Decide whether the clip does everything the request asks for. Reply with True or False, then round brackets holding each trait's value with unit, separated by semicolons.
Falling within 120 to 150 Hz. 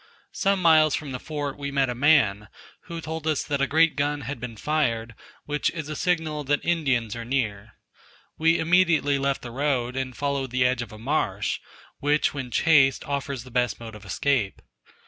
True (140 Hz)